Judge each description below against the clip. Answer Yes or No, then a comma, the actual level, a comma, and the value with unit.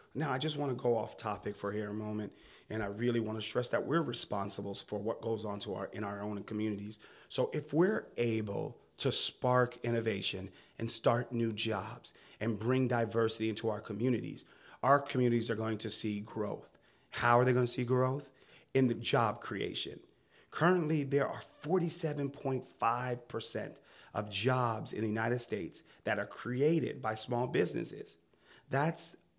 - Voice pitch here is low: Yes, low, 115 Hz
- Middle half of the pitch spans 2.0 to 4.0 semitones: Yes, average, 3.2 semitones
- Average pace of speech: Yes, average, 170 wpm